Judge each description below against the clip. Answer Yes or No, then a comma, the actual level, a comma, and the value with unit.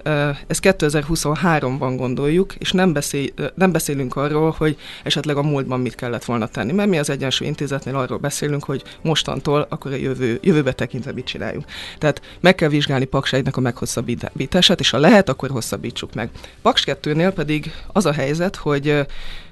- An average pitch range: Yes, average, 3.3 semitones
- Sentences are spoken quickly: Yes, fast, 165 wpm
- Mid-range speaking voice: Yes, medium, 145 Hz